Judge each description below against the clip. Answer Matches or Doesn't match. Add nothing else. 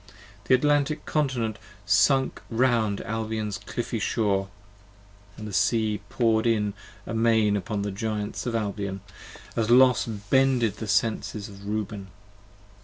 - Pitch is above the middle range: Doesn't match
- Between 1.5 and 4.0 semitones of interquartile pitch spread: Matches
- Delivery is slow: Matches